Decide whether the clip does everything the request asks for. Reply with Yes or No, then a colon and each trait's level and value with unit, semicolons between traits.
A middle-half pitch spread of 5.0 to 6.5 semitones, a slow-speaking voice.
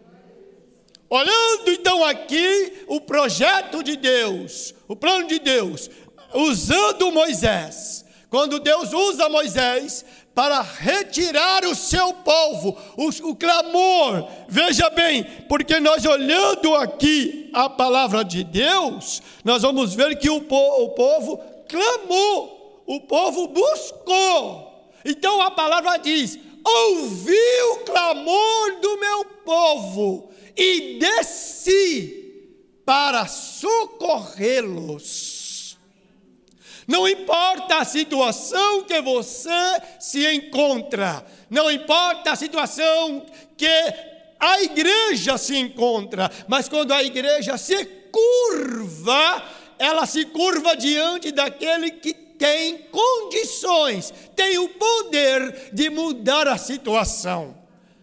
Yes: average, 5.3 semitones; slow, 100 wpm